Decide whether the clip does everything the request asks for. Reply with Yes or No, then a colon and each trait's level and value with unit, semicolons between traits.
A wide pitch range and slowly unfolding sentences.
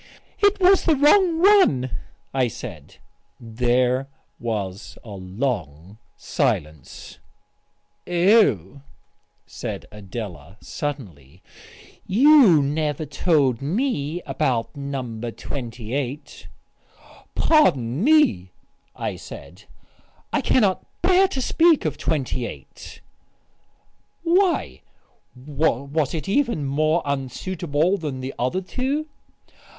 Yes: wide, 9.0 semitones; slow, 90 wpm